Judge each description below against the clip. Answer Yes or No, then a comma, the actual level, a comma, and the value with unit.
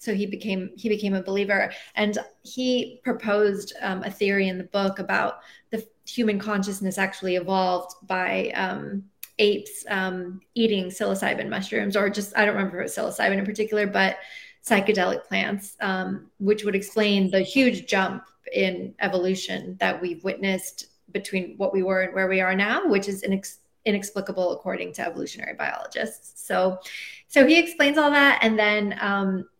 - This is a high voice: Yes, high, 200 Hz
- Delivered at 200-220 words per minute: No, average, 165 wpm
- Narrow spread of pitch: Yes, narrow, 1.9 semitones